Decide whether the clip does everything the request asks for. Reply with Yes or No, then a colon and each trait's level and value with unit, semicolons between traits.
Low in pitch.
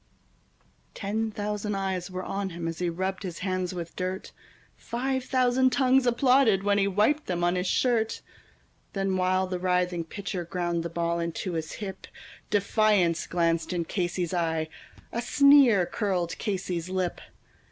No: medium, 185 Hz